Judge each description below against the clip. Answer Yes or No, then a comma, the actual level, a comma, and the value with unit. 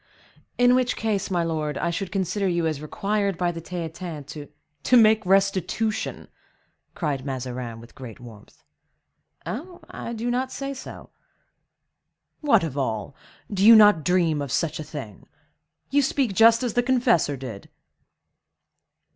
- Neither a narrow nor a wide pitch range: No, wide, 7.0 semitones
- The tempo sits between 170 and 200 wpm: No, average, 145 wpm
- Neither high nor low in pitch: Yes, medium, 180 Hz